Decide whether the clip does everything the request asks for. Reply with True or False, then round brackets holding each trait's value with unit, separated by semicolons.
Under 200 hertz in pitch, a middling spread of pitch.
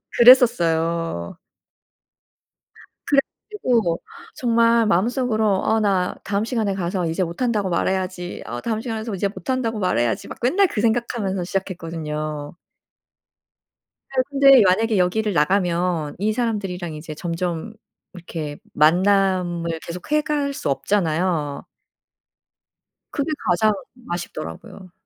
True (190 Hz; 5.0 semitones)